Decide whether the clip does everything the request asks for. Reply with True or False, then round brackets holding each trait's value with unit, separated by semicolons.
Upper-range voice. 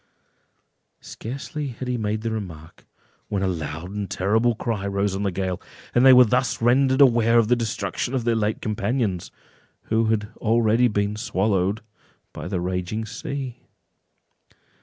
False (110 Hz)